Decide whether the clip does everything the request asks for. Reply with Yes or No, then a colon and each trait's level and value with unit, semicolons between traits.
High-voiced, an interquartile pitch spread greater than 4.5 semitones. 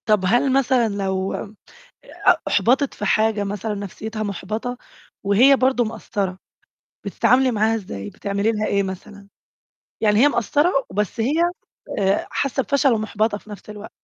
No: high, 215 Hz; average, 3.2 semitones